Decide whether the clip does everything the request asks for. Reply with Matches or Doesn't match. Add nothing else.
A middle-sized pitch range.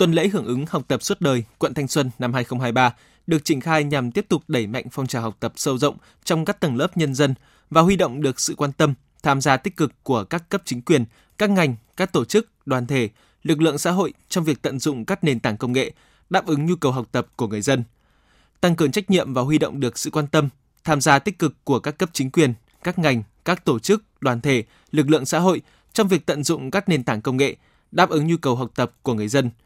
Matches